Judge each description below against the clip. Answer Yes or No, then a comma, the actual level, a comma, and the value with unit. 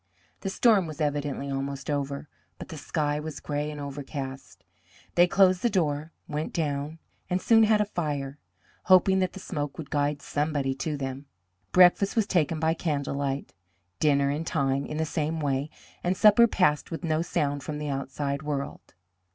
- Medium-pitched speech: Yes, medium, 150 Hz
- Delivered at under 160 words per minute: No, average, 175 wpm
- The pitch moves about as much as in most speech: Yes, average, 3.4 semitones